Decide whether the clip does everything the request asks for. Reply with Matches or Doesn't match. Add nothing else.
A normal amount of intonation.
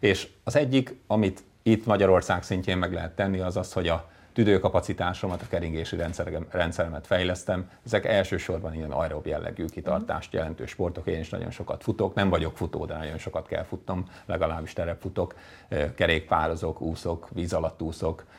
Matches